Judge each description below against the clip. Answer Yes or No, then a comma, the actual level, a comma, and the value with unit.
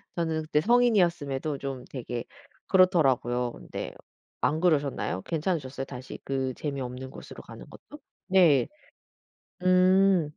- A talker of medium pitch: Yes, medium, 150 Hz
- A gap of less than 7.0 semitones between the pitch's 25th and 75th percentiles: Yes, wide, 5.6 semitones